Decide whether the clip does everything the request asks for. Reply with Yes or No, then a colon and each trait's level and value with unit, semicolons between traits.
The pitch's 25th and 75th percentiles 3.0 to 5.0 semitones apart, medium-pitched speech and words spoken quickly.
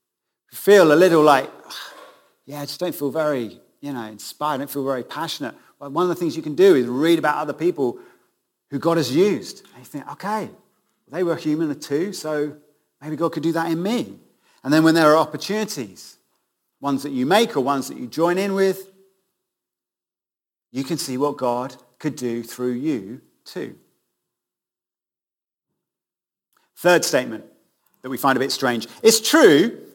No: average, 4.6 semitones; medium, 150 Hz; average, 180 wpm